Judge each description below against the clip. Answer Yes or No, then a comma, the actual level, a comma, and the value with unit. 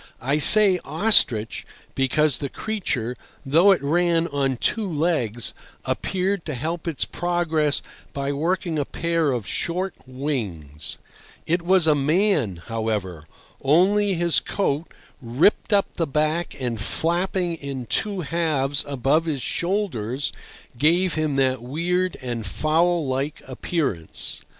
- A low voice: No, medium, 155 Hz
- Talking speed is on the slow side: Yes, slow, 125 wpm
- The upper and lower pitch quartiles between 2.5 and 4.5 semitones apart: No, average, 4.9 semitones